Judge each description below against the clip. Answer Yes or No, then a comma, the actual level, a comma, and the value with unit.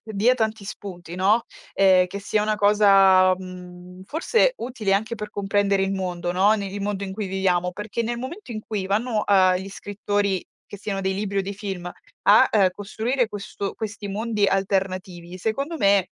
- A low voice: No, high, 200 Hz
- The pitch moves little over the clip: Yes, narrow, 2.2 semitones